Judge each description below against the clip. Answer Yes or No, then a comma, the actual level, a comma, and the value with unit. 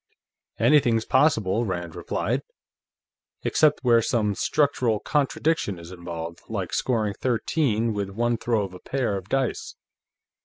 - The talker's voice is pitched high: No, low, 115 Hz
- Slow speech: Yes, slow, 125 wpm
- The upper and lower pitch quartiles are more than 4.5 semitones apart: Yes, average, 5.0 semitones